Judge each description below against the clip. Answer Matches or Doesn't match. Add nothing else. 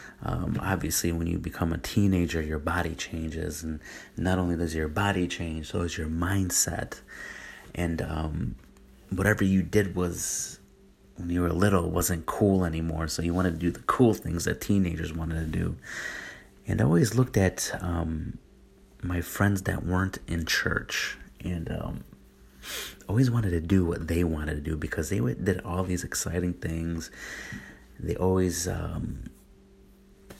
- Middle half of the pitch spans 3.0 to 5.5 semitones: Doesn't match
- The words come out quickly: Doesn't match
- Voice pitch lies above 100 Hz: Doesn't match